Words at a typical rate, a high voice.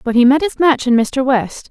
No: fast, 280 wpm; very high, 260 Hz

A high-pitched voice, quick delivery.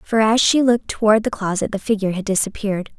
Yes: high, 210 Hz; fast, 220 wpm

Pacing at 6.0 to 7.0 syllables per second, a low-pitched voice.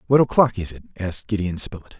Yes: 6.9 syllables/s; low, 100 Hz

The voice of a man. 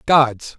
Yes: male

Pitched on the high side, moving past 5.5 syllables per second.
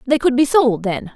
No: very high, 250 Hz; 5.0 syllables/s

